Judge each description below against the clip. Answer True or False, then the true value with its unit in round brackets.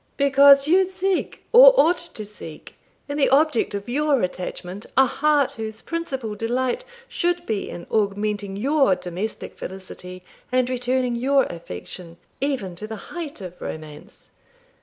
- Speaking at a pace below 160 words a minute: True (140 wpm)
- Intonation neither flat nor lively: False (6.5 semitones)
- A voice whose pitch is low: False (245 Hz)